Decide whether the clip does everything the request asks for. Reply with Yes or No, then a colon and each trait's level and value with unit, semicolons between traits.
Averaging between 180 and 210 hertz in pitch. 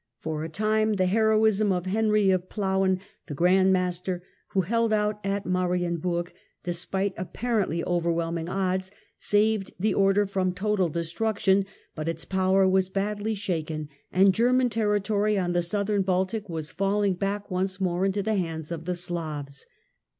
Yes: high, 190 Hz